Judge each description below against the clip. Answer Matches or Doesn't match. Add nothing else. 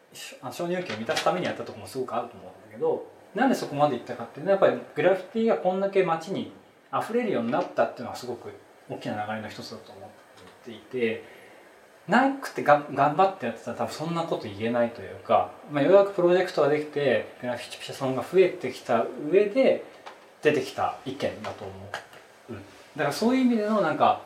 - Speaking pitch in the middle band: Matches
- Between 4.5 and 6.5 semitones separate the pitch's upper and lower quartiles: Doesn't match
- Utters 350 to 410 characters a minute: Doesn't match